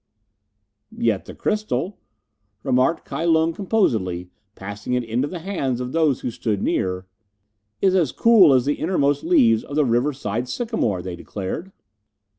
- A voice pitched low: Yes, low, 130 Hz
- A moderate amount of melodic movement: No, wide, 7.3 semitones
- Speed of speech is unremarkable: Yes, average, 150 wpm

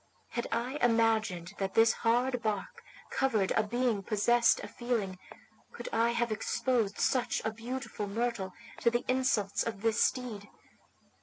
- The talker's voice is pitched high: Yes, high, 230 Hz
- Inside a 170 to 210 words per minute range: No, average, 145 wpm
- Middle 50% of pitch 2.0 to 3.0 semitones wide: Yes, narrow, 2.6 semitones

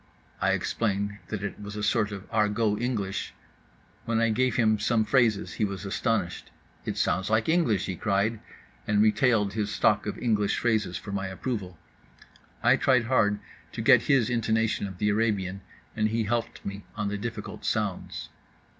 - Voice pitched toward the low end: Yes, low, 105 Hz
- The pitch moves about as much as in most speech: No, narrow, 2.0 semitones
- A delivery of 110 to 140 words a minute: No, average, 165 wpm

